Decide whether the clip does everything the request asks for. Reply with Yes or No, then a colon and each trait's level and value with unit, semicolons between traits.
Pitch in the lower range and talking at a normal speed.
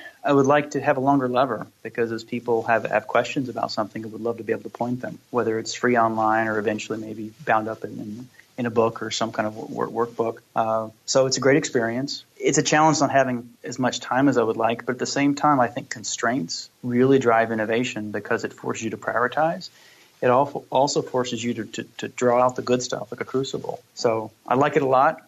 No: low, 120 Hz; fast, 240 wpm